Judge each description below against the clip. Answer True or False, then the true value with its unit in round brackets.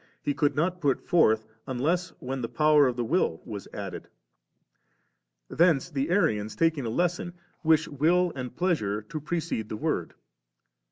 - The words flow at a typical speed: True (160 wpm)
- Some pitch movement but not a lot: False (5.8 semitones)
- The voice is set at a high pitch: False (145 Hz)